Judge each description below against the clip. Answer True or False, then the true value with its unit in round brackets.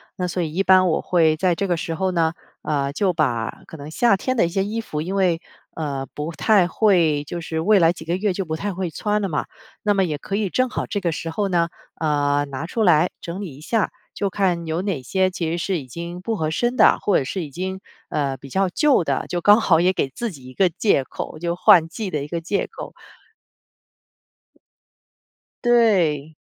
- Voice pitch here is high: False (175 Hz)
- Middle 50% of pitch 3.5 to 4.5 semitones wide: True (3.8 semitones)